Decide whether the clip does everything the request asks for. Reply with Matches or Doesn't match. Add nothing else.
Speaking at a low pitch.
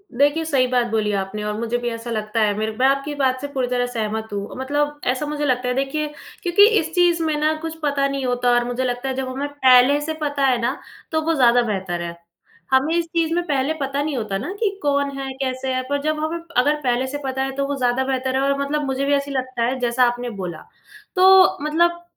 Doesn't match